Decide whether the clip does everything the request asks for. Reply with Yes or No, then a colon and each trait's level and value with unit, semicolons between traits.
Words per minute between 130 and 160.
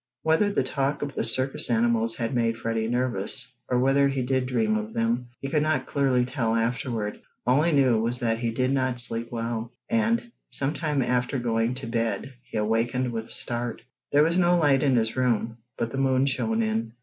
No: fast, 205 wpm